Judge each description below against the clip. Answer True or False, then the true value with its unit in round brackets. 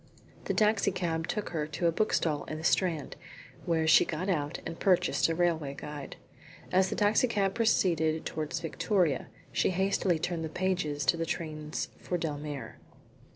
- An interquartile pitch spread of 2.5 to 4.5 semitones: True (3.3 semitones)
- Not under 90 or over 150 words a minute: False (165 wpm)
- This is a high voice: False (165 Hz)